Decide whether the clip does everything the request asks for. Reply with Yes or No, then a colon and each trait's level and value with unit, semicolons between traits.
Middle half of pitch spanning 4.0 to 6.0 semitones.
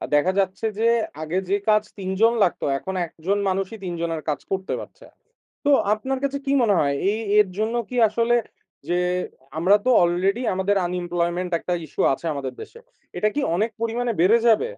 Yes: average, 4.5 semitones